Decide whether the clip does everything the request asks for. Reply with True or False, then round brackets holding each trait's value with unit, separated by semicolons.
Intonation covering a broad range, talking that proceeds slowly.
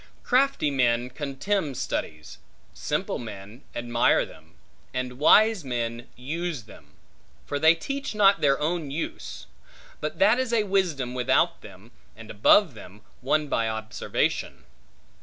True (7.0 semitones; 130 wpm)